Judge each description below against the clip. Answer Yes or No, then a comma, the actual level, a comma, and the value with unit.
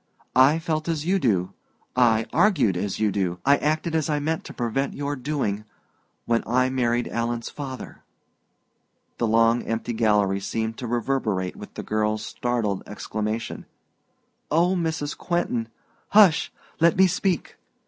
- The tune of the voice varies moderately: No, wide, 5.9 semitones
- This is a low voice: Yes, low, 120 Hz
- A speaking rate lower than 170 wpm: Yes, average, 150 wpm